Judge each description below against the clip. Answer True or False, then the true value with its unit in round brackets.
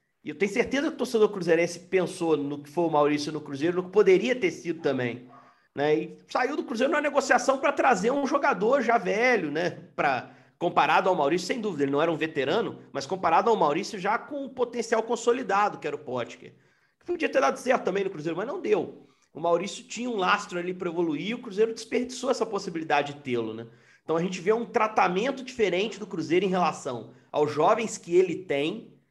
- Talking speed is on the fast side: True (210 wpm)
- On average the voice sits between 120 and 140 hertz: False (200 Hz)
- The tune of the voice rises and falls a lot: True (6.9 semitones)